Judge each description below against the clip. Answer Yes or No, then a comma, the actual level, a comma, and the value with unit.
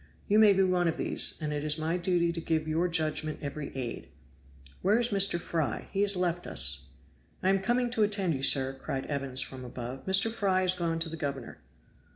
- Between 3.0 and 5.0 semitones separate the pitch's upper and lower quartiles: Yes, average, 4.6 semitones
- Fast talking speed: Yes, fast, 210 wpm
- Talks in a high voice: No, medium, 170 Hz